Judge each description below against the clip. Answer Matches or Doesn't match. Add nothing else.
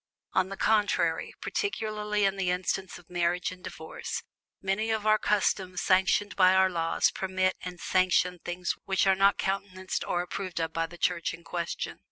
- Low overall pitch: Doesn't match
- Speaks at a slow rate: Doesn't match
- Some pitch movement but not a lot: Doesn't match